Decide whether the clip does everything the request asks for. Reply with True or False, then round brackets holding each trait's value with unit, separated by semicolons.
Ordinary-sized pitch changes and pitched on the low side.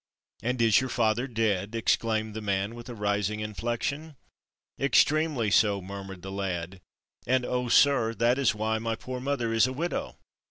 True (3.4 semitones; 115 Hz)